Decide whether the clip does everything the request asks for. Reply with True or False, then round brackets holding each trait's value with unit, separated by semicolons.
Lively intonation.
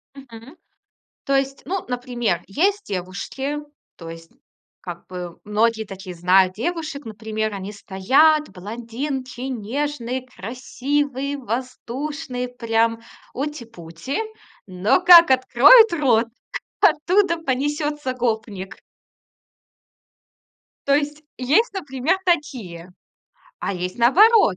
True (5.9 semitones)